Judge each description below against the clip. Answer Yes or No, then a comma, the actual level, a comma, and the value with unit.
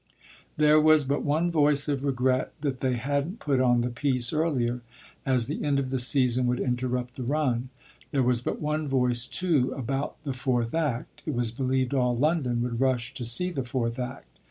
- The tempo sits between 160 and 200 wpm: Yes, average, 195 wpm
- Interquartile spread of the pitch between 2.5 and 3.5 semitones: Yes, average, 2.9 semitones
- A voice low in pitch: Yes, low, 130 Hz